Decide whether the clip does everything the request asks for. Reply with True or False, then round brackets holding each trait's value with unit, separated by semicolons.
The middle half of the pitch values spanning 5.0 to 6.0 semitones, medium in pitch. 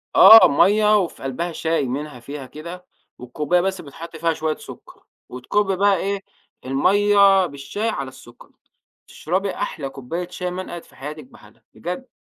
True (5.5 semitones; 170 Hz)